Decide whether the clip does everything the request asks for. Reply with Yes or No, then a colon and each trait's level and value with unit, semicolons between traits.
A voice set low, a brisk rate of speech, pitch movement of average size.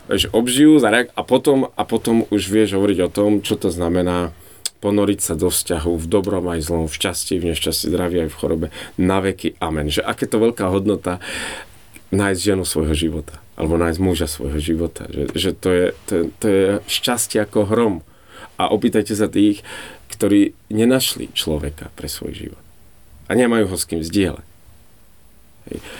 Yes: very low, 95 Hz; fast, 170 wpm; average, 4.1 semitones